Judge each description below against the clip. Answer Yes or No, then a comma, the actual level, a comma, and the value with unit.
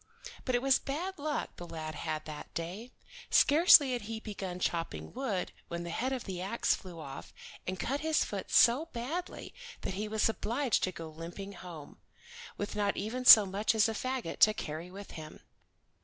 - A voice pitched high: Yes, high, 210 Hz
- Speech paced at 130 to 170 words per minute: No, average, 185 wpm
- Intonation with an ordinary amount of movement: No, wide, 6.4 semitones